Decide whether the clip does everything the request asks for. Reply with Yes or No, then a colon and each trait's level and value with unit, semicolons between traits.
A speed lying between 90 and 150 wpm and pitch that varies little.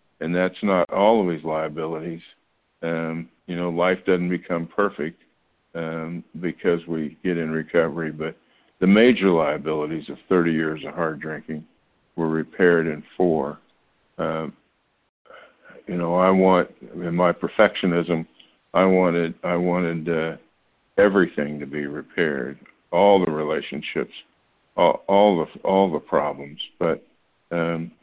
Yes: slow, 135 wpm; narrow, 1.9 semitones